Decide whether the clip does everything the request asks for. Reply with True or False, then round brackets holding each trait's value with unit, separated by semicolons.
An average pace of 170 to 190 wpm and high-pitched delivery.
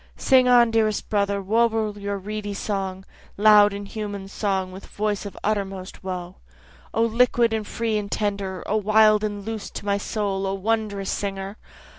False (160 wpm; 205 Hz)